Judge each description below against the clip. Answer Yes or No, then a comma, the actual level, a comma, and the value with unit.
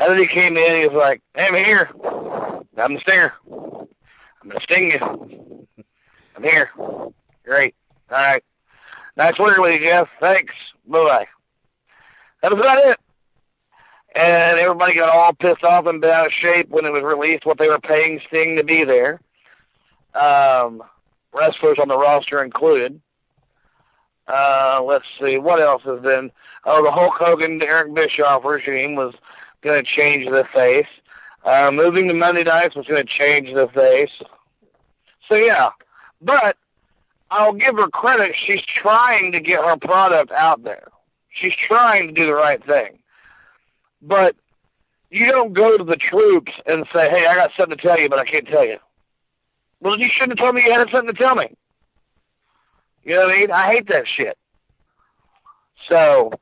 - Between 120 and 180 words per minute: Yes, average, 170 wpm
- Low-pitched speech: No, medium, 170 Hz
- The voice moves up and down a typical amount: No, wide, 6.3 semitones